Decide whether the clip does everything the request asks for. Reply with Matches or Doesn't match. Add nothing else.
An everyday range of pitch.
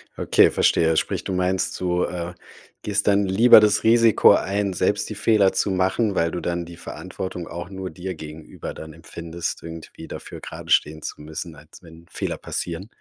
Matches